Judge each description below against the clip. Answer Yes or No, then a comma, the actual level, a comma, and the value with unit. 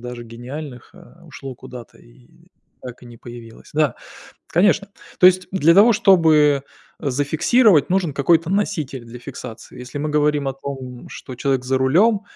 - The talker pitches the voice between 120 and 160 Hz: Yes, medium, 140 Hz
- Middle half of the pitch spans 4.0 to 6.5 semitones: Yes, average, 5.2 semitones